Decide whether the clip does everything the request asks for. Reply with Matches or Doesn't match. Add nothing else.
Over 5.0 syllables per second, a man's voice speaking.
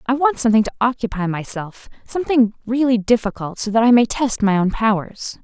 Doesn't match